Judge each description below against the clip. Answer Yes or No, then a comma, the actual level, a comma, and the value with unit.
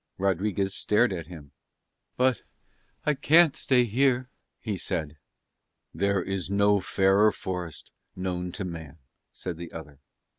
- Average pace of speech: No, slow, 125 wpm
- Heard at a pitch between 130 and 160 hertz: No, very low, 95 Hz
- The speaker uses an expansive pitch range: No, average, 3.8 semitones